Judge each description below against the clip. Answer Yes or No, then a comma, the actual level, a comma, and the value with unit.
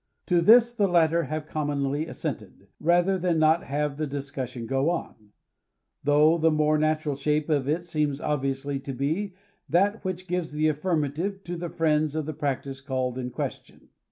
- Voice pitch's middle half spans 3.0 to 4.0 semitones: Yes, average, 3.4 semitones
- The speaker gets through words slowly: No, average, 170 wpm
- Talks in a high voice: No, medium, 155 Hz